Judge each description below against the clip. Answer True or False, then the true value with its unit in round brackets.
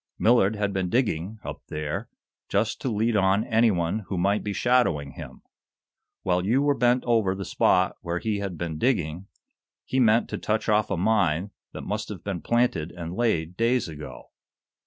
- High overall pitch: False (100 Hz)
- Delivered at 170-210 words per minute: True (180 wpm)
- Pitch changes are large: False (4.5 semitones)